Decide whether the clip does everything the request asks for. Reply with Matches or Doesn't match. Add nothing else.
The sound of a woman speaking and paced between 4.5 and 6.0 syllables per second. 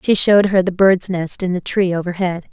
Matches